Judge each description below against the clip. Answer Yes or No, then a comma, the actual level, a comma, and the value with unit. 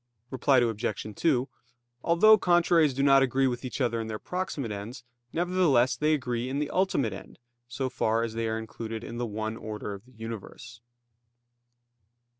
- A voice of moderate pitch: No, low, 120 Hz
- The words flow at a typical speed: Yes, average, 170 wpm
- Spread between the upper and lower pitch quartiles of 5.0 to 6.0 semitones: No, average, 3.9 semitones